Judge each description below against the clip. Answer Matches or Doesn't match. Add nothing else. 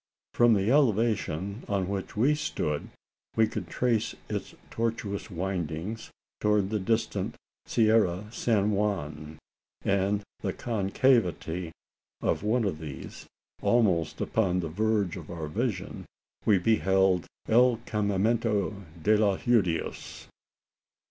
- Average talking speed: Doesn't match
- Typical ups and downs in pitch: Matches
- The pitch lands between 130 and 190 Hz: Doesn't match